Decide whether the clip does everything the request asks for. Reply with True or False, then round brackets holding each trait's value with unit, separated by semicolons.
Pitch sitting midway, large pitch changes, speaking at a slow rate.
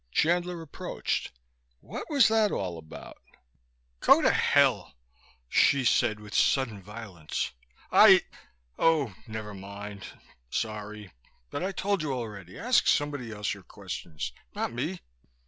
False (110 Hz; 7.6 semitones; 125 wpm)